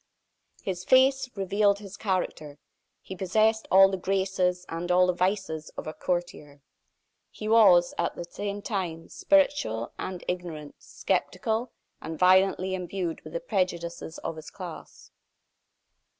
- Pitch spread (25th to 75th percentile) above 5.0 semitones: No, average, 2.8 semitones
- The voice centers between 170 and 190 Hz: Yes, medium, 185 Hz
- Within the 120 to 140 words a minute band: Yes, slow, 135 wpm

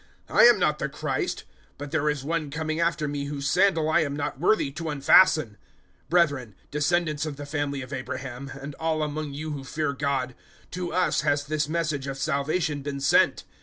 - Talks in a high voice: No, medium, 150 Hz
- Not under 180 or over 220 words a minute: Yes, average, 195 wpm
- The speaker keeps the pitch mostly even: Yes, narrow, 2.1 semitones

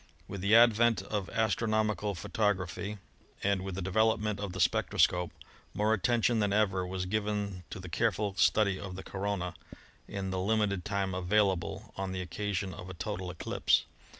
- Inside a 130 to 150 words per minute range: No, average, 175 wpm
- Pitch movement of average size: No, narrow, 2.3 semitones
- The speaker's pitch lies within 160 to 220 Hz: No, low, 100 Hz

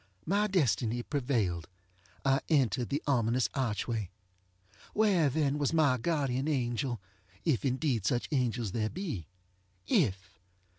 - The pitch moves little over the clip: No, average, 5.0 semitones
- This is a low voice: Yes, low, 130 Hz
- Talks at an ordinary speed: No, slow, 110 wpm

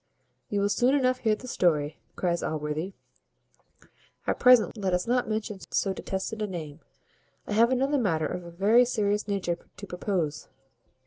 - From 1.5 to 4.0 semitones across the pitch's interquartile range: No, average, 4.9 semitones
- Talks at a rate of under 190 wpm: Yes, average, 165 wpm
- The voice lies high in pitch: Yes, high, 200 Hz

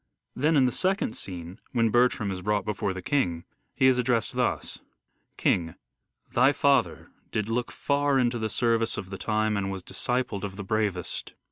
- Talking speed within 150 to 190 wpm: Yes, average, 175 wpm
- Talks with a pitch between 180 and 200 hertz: No, low, 110 Hz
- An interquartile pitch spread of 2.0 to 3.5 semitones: No, average, 4.5 semitones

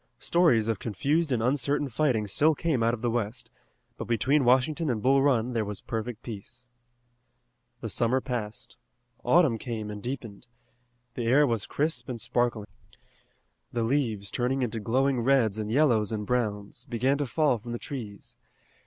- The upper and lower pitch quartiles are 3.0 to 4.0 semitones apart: Yes, average, 3.4 semitones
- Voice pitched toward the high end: No, low, 120 Hz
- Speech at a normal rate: Yes, average, 160 wpm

